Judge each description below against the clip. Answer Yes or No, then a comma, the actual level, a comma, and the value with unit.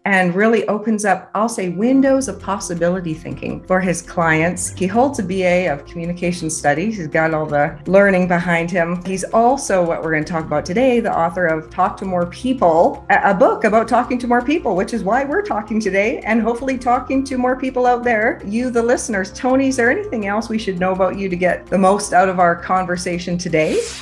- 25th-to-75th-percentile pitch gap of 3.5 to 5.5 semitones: Yes, average, 5.2 semitones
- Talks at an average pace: No, fast, 215 wpm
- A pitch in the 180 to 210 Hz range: Yes, high, 190 Hz